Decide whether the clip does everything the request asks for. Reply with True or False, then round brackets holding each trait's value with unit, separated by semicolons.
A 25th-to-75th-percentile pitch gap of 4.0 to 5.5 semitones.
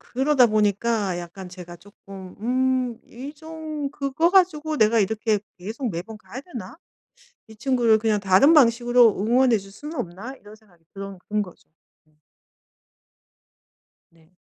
True (5.2 semitones)